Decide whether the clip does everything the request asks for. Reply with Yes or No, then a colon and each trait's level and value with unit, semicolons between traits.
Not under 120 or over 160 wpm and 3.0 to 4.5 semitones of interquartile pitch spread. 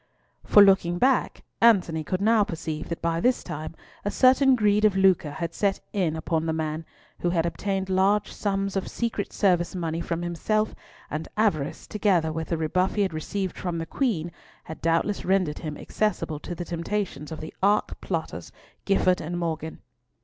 No: average, 180 wpm; average, 3.9 semitones